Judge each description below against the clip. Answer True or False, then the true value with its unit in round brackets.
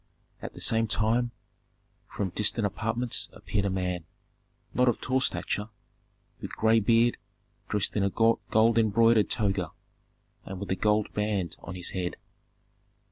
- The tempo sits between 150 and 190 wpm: False (140 wpm)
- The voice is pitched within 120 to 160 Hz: False (105 Hz)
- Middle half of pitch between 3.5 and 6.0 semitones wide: False (2.6 semitones)